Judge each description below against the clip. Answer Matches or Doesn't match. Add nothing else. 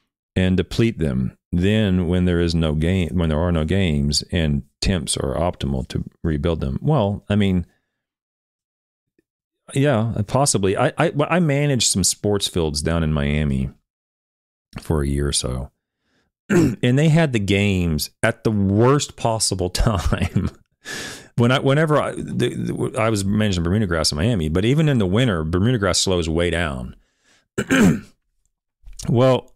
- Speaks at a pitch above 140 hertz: Doesn't match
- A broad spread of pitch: Matches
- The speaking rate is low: Doesn't match